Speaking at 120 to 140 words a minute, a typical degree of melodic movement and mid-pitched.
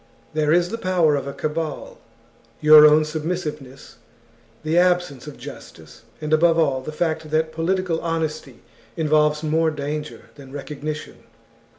No: slow, 135 wpm; narrow, 1.6 semitones; medium, 155 Hz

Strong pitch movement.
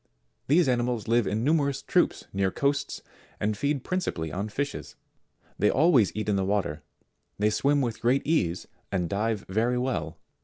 Yes: wide, 5.8 semitones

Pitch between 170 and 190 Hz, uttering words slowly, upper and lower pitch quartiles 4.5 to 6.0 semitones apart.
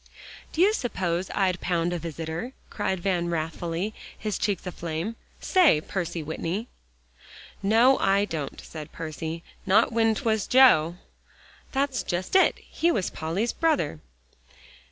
Yes: medium, 185 Hz; slow, 130 wpm; wide, 5.4 semitones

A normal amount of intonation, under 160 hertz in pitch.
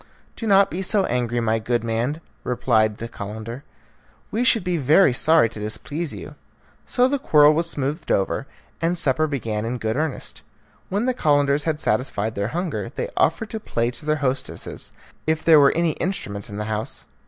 No: wide, 6.6 semitones; medium, 140 Hz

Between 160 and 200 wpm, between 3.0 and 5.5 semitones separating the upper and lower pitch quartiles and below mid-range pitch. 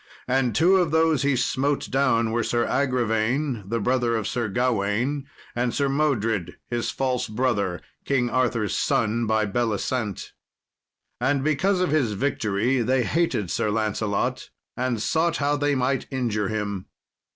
No: average, 145 wpm; average, 4.0 semitones; low, 125 Hz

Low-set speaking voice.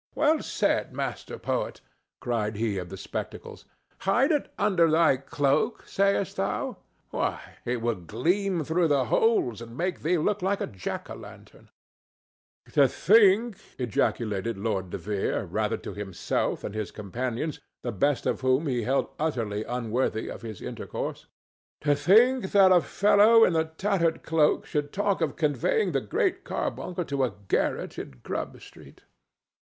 No: medium, 145 Hz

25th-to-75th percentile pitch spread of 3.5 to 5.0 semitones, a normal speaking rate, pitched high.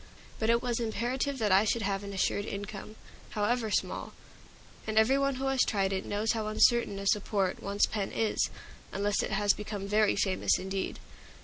No: narrow, 2.6 semitones; average, 185 wpm; high, 210 Hz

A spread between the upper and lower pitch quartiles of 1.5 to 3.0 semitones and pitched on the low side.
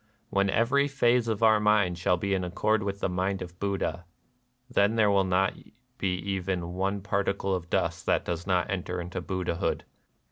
Yes: narrow, 2.4 semitones; very low, 95 Hz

